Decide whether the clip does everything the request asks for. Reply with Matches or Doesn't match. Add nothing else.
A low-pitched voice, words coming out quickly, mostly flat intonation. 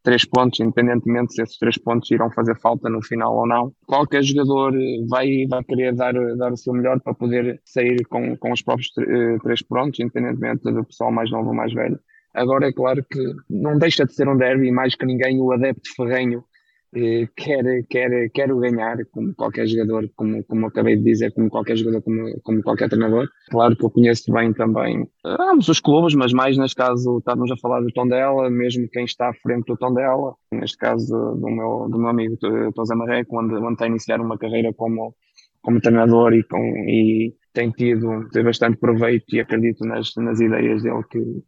Matches